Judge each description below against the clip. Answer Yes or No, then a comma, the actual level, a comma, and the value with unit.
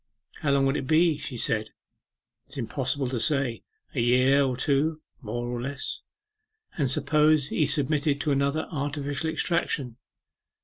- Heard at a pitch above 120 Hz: Yes, medium, 140 Hz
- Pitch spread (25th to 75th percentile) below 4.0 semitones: Yes, average, 2.7 semitones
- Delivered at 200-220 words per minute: No, average, 150 wpm